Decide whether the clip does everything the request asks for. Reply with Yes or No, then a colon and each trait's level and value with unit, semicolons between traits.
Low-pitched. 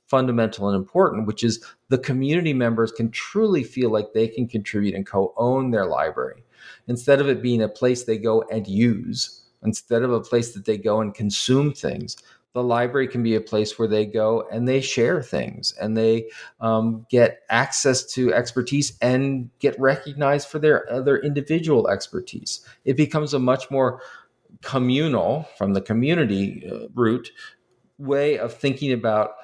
Yes: low, 120 Hz